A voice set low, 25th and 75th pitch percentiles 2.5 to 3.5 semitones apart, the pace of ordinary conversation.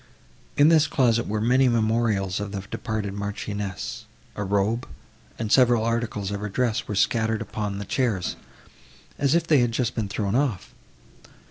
Yes: low, 110 Hz; average, 3.1 semitones; average, 160 wpm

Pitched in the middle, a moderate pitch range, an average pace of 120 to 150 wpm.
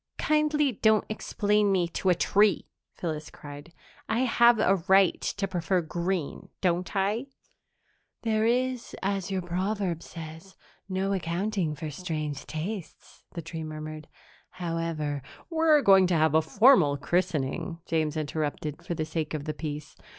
Yes: medium, 180 Hz; average, 4.5 semitones; average, 145 wpm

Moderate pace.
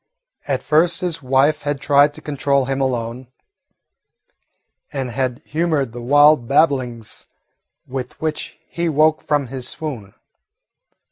No: slow, 125 wpm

